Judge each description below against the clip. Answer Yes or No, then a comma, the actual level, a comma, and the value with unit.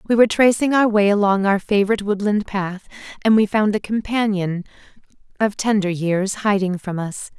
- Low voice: No, high, 205 Hz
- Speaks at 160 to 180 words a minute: Yes, average, 170 wpm